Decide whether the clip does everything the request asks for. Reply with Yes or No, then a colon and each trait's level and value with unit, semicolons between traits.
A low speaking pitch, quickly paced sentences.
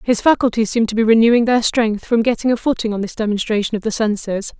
No: high, 225 Hz; fast, 235 wpm